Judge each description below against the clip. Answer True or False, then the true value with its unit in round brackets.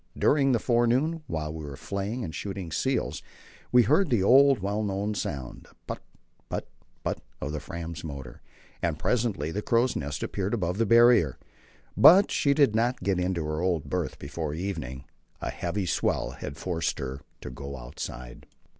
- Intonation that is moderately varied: False (7.4 semitones)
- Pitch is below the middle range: True (95 Hz)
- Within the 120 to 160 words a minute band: False (170 wpm)